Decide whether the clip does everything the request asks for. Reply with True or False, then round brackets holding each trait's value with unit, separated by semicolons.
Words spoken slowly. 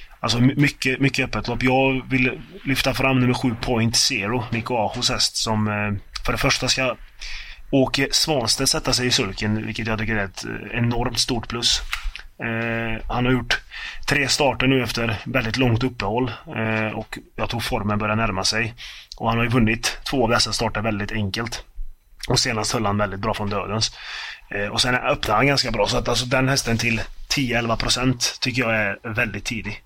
False (180 wpm)